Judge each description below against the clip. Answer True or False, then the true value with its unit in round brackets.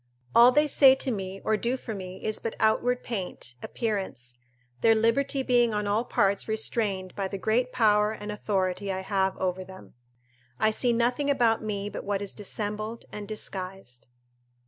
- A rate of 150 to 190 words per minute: True (170 wpm)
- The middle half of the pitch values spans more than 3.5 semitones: False (3.2 semitones)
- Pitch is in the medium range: False (210 Hz)